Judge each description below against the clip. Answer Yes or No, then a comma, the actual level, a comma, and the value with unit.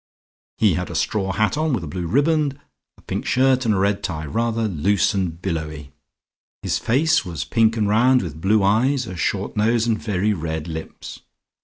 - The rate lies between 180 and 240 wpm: Yes, average, 190 wpm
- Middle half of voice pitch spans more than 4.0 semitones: Yes, average, 5.3 semitones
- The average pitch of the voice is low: Yes, low, 105 Hz